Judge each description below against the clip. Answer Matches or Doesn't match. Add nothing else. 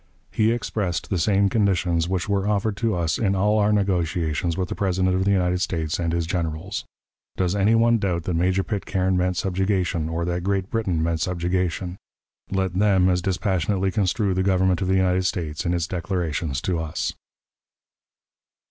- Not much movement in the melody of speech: Matches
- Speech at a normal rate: Matches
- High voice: Doesn't match